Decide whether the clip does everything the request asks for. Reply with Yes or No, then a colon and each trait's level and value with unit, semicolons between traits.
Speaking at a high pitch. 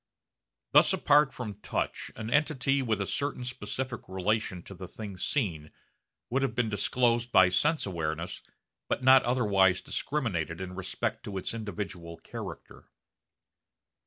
No: low, 110 Hz